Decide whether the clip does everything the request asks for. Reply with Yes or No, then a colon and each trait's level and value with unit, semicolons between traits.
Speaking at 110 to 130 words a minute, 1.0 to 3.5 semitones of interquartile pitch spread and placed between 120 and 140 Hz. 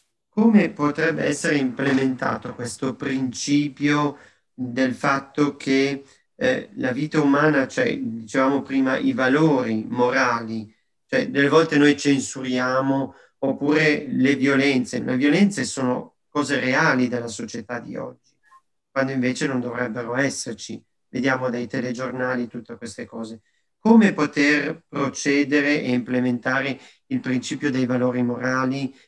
Yes: average, 120 wpm; narrow, 2.5 semitones; low, 135 Hz